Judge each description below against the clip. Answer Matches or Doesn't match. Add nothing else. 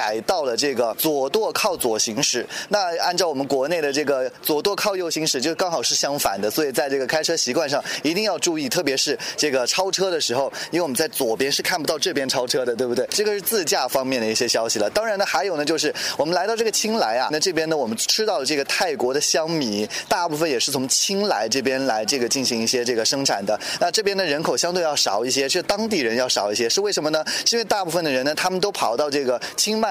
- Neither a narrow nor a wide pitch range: Doesn't match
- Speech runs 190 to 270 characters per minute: Doesn't match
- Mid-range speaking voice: Matches